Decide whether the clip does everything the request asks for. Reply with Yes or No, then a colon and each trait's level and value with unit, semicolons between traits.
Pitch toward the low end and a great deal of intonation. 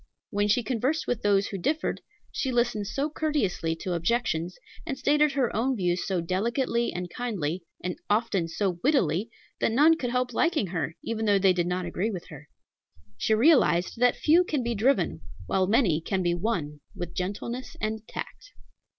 No: high, 210 Hz; wide, 5.8 semitones